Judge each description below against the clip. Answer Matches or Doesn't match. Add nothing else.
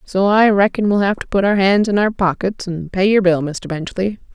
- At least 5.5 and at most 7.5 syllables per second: Doesn't match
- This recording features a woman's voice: Matches